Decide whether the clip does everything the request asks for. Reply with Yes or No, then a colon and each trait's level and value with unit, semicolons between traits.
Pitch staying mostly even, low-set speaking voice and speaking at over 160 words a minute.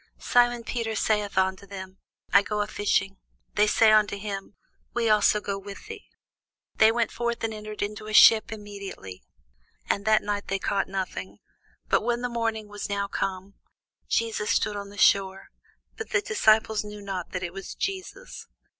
No: narrow, 2.0 semitones; high, 210 Hz; average, 170 wpm